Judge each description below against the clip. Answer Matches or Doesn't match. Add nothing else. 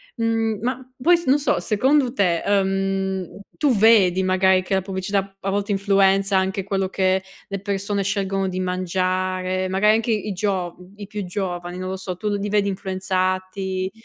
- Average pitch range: Doesn't match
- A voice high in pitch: Matches